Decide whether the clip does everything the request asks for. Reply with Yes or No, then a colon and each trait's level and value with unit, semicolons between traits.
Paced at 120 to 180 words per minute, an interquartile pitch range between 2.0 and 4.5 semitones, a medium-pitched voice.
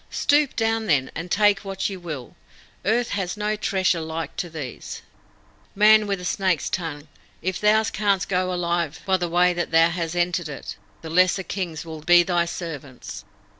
Yes: average, 175 wpm; average, 3.2 semitones; medium, 175 Hz